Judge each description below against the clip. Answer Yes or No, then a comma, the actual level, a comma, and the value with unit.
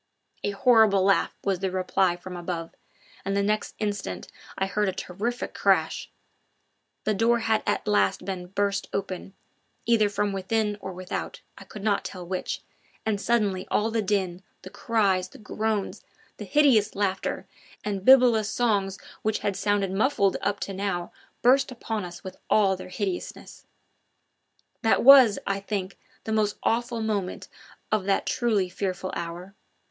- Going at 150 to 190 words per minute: Yes, average, 155 wpm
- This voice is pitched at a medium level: No, high, 200 Hz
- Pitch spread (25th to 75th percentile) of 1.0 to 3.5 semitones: Yes, narrow, 2.4 semitones